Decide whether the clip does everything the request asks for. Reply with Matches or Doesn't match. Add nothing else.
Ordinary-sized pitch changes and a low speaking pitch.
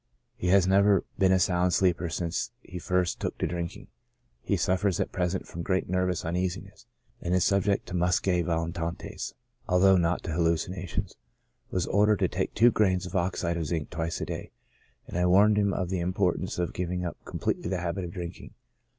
Doesn't match